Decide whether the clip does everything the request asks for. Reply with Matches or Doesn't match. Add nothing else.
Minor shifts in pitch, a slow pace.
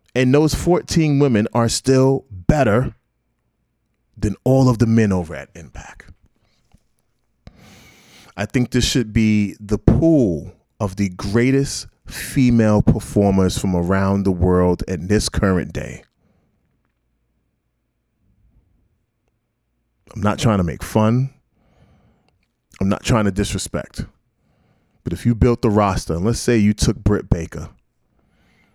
Doesn't match